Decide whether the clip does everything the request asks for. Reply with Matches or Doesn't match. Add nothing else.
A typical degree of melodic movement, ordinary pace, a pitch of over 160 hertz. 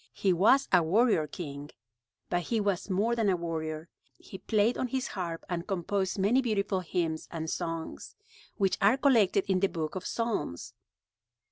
Matches